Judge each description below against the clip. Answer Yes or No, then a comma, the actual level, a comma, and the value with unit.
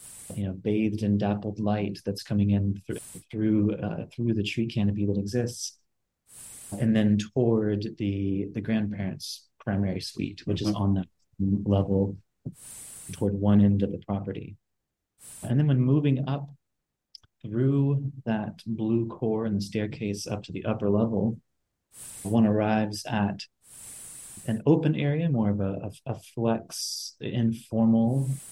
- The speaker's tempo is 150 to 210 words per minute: No, average, 140 wpm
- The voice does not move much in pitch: Yes, narrow, 2.3 semitones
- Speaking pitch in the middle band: No, low, 105 Hz